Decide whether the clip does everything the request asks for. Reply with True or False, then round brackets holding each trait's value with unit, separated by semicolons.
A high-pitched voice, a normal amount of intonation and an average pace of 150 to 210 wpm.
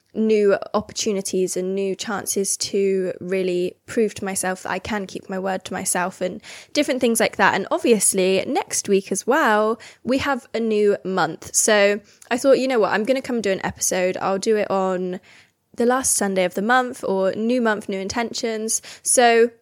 True (205 Hz; 3.4 semitones; 195 wpm)